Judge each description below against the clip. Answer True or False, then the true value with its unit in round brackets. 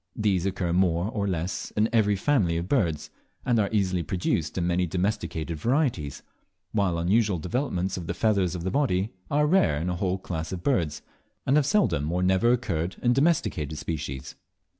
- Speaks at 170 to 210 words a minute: True (180 wpm)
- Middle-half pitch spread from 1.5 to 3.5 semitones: False (4.6 semitones)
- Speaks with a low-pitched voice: True (95 Hz)